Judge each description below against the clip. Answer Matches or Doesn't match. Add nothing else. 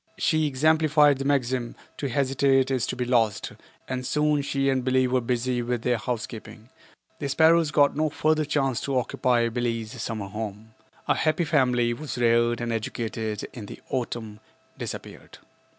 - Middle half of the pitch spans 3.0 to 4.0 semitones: Matches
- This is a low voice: Matches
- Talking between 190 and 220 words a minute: Doesn't match